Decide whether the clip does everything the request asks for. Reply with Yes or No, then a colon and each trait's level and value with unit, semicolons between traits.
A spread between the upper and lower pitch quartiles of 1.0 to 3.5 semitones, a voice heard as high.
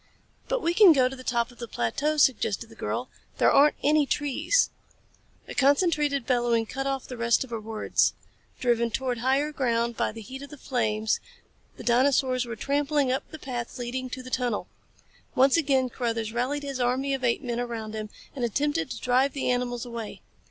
Yes: average, 2.9 semitones; very high, 255 Hz